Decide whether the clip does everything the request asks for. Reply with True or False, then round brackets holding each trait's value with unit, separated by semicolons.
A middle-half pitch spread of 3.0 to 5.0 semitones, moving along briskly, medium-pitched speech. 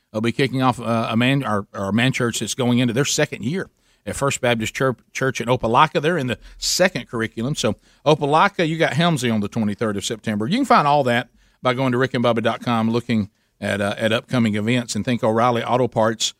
False (3.3 semitones; 210 wpm; 120 Hz)